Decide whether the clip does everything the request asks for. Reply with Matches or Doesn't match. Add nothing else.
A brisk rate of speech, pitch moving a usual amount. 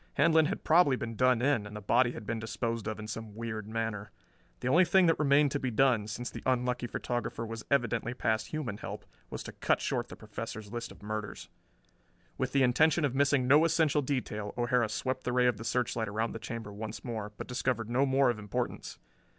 Matches